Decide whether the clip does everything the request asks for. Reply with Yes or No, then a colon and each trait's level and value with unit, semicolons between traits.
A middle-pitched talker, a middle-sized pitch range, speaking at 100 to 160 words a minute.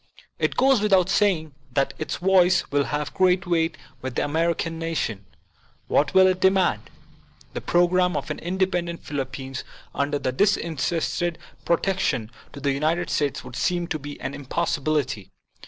Yes: medium, 165 Hz; average, 4.0 semitones; average, 155 wpm